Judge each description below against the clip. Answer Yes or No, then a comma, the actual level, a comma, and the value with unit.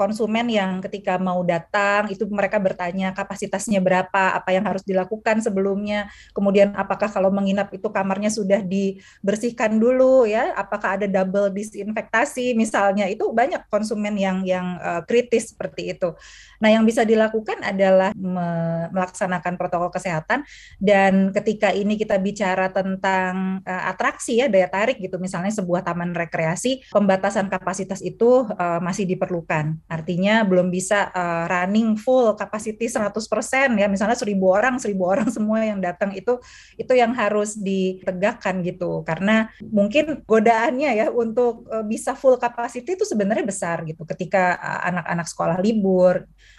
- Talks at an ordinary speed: No, fast, 145 wpm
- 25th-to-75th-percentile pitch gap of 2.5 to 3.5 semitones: Yes, average, 2.9 semitones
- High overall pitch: Yes, high, 200 Hz